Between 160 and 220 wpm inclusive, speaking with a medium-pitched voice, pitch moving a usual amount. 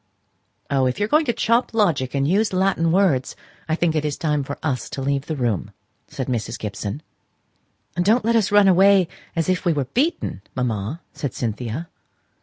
No: average, 190 wpm; medium, 160 Hz; wide, 6.8 semitones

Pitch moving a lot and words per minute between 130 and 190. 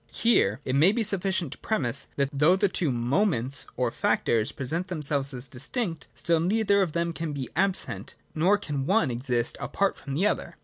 No: wide, 6.4 semitones; fast, 205 wpm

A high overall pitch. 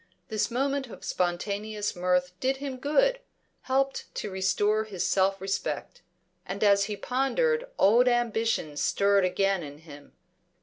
Yes: high, 210 Hz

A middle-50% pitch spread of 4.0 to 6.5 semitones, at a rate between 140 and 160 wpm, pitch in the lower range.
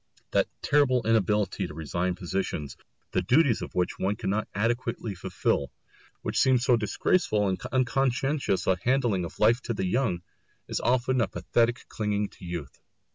Yes: average, 4.9 semitones; average, 155 wpm; low, 110 Hz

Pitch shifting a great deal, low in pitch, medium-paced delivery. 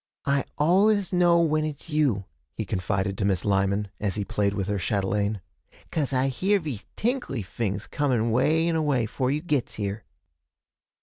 Yes: wide, 7.4 semitones; low, 125 Hz; average, 170 wpm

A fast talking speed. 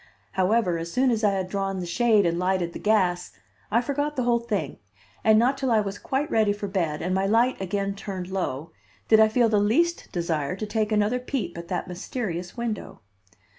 Yes: fast, 210 wpm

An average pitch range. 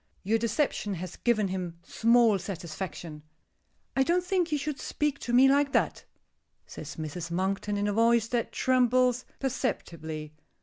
No: wide, 5.9 semitones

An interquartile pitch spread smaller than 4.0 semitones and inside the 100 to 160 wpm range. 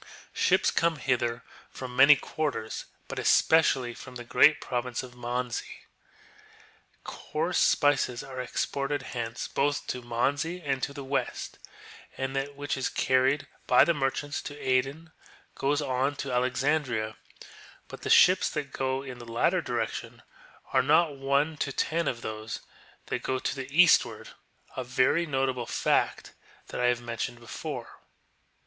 Yes: average, 2.7 semitones; average, 150 wpm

